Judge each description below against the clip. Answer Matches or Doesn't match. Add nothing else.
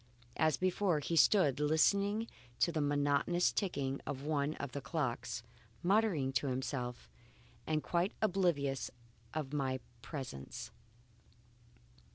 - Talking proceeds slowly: Matches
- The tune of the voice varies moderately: Matches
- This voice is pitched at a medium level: Matches